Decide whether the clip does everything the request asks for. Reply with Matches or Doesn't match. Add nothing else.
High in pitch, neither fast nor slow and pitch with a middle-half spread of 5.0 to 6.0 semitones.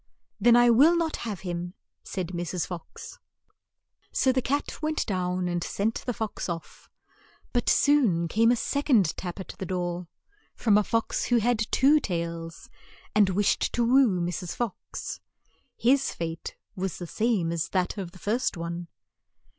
Matches